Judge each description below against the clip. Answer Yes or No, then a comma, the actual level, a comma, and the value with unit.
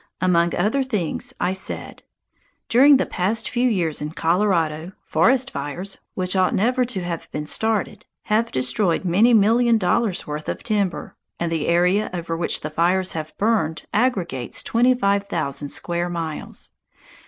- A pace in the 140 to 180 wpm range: Yes, average, 155 wpm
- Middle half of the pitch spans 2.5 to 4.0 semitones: No, average, 4.9 semitones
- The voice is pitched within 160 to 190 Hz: Yes, medium, 185 Hz